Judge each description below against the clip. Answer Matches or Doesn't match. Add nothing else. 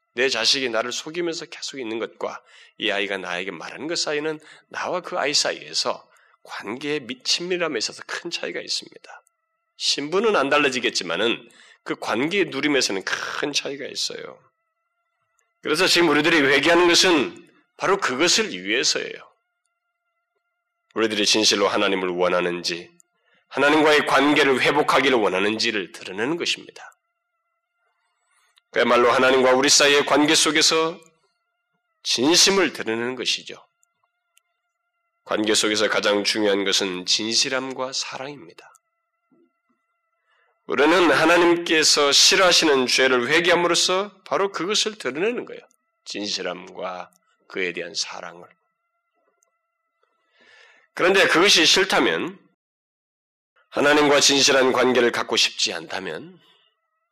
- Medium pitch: Matches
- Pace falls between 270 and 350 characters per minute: Matches